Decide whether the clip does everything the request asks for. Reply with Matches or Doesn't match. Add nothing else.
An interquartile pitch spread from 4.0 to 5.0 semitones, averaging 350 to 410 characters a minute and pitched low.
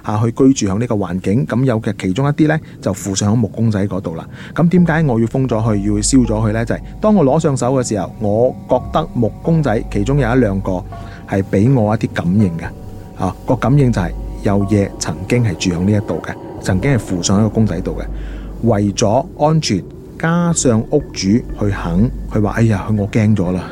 Doesn't match